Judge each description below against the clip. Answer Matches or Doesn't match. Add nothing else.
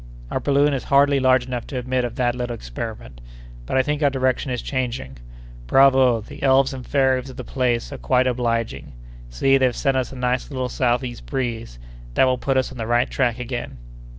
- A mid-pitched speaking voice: Doesn't match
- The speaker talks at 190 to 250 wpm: Matches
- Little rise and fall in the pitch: Matches